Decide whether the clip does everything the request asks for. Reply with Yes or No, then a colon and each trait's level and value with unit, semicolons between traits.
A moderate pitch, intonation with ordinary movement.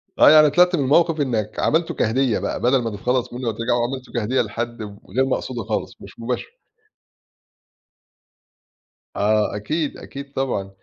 No: low, 125 Hz; average, 3.7 semitones